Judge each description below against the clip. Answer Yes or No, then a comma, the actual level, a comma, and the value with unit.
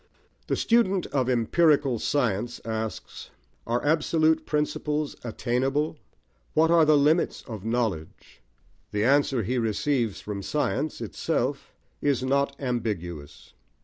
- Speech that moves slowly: Yes, slow, 115 wpm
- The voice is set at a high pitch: No, low, 130 Hz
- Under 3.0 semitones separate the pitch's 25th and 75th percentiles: No, average, 5.0 semitones